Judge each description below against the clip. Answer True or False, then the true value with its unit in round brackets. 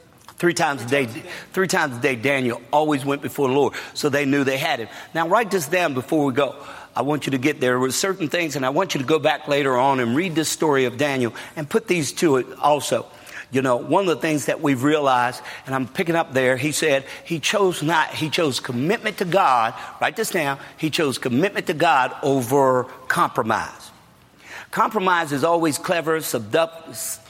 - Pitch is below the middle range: False (145 Hz)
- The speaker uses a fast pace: True (215 wpm)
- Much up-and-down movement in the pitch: False (3.7 semitones)